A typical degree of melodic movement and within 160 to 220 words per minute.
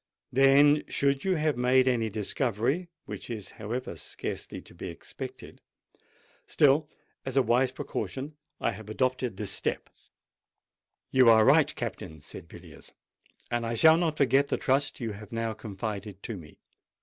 No: average, 4.1 semitones; average, 145 wpm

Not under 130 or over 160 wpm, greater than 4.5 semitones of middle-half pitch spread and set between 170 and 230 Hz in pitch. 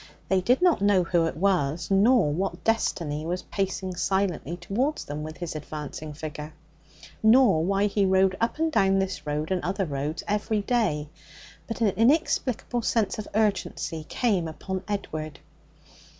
Yes: average, 155 wpm; average, 5.0 semitones; high, 190 Hz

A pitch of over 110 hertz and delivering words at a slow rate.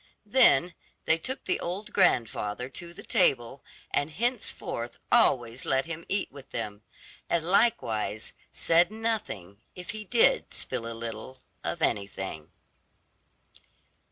Yes: medium, 140 Hz; slow, 125 wpm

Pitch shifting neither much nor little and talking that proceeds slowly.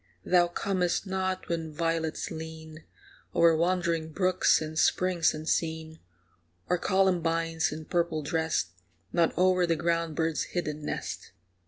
No: narrow, 1.9 semitones; slow, 125 wpm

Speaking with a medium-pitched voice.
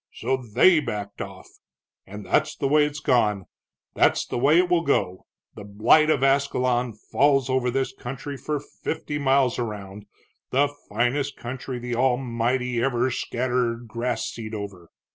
No: low, 125 Hz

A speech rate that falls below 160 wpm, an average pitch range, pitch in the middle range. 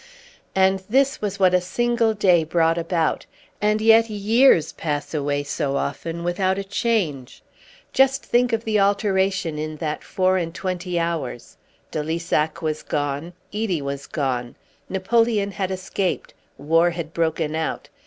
Yes: average, 145 wpm; average, 4.4 semitones; medium, 180 Hz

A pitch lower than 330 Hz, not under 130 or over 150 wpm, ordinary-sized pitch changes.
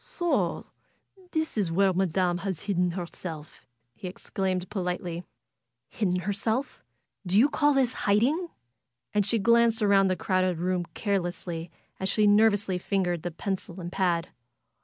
Yes: high, 190 Hz; average, 145 wpm; average, 3.0 semitones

